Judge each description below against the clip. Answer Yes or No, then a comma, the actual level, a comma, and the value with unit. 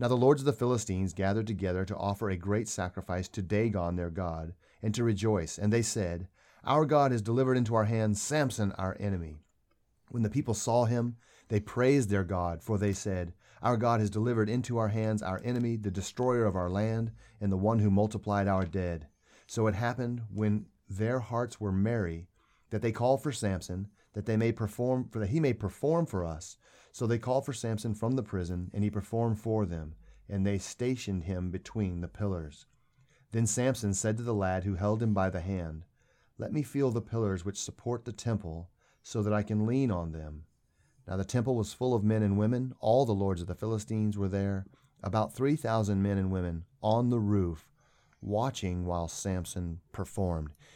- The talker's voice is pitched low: Yes, low, 105 Hz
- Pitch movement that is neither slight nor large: Yes, average, 3.7 semitones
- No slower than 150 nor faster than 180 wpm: No, average, 200 wpm